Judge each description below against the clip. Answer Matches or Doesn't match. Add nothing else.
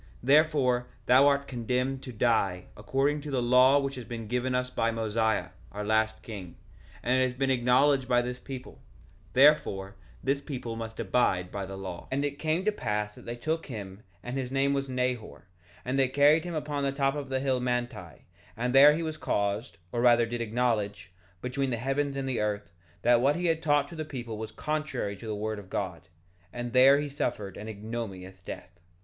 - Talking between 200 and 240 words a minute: Matches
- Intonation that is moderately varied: Matches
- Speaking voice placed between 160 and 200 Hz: Doesn't match